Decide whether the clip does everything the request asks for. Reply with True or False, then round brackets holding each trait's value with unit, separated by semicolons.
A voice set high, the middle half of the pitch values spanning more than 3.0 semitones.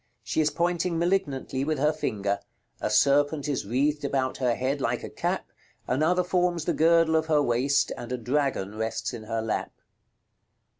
False (145 Hz; 4.6 semitones)